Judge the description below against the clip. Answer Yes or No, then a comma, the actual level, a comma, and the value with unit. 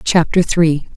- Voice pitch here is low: No, medium, 165 Hz